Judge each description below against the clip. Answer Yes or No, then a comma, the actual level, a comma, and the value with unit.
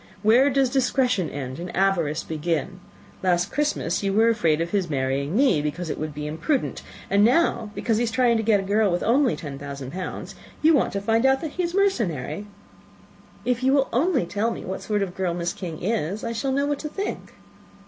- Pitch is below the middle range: No, high, 205 Hz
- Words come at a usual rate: No, fast, 215 wpm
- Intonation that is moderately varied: No, wide, 7.2 semitones